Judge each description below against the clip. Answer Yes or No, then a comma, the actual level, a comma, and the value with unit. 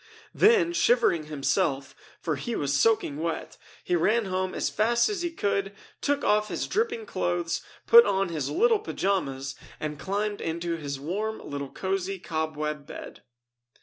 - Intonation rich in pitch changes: Yes, wide, 7.0 semitones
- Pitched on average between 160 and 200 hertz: Yes, medium, 185 Hz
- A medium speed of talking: Yes, average, 150 wpm